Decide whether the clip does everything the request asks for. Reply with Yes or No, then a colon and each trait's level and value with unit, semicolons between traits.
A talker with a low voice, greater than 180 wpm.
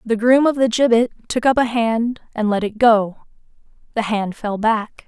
No: high, 230 Hz; average, 200 wpm